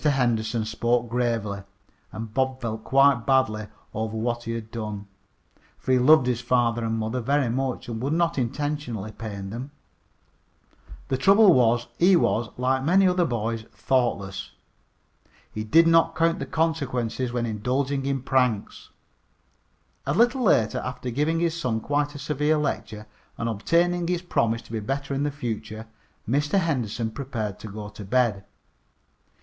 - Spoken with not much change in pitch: No, average, 4.5 semitones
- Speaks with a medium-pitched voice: No, low, 125 Hz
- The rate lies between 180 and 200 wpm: No, average, 155 wpm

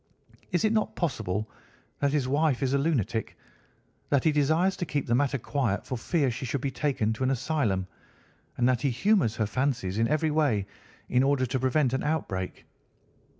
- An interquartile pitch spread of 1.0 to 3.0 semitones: No, average, 4.2 semitones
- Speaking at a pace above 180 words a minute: Yes, average, 190 wpm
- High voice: No, low, 135 Hz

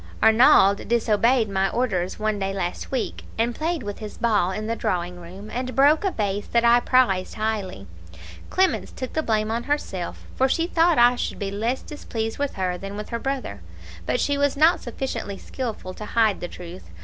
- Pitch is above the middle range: Yes, high, 220 Hz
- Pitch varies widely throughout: No, average, 4.7 semitones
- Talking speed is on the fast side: No, average, 195 wpm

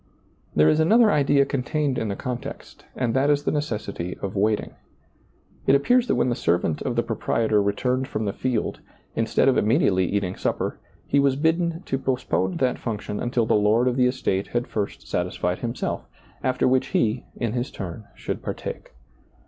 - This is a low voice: Yes, low, 120 Hz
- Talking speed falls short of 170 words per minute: No, average, 180 wpm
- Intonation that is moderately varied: Yes, average, 4.6 semitones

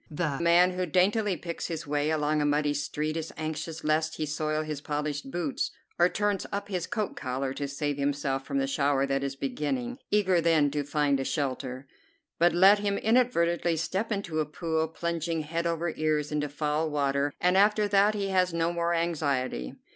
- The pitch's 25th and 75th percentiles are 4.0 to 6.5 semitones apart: No, average, 3.3 semitones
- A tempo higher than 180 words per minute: Yes, average, 190 wpm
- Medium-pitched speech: Yes, medium, 155 Hz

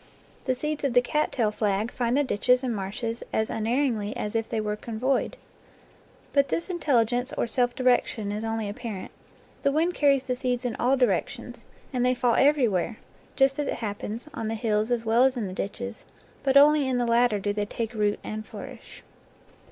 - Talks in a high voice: Yes, high, 240 Hz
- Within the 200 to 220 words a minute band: Yes, fast, 205 wpm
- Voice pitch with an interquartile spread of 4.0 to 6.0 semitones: No, average, 3.3 semitones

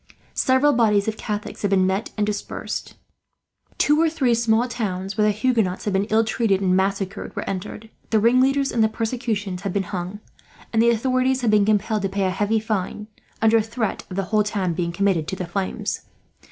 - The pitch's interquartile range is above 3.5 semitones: No, average, 2.8 semitones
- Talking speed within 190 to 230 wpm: Yes, average, 200 wpm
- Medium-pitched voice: No, high, 210 Hz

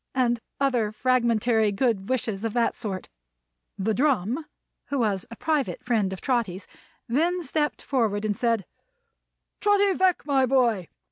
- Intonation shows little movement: No, average, 4.3 semitones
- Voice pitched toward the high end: Yes, high, 235 Hz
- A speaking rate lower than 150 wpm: Yes, average, 140 wpm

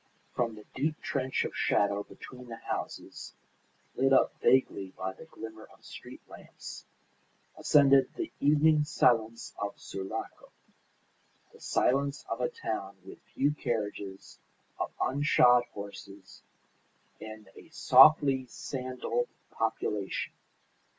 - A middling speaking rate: No, slow, 115 wpm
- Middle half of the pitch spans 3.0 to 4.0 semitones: No, average, 4.7 semitones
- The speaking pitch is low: Yes, low, 125 Hz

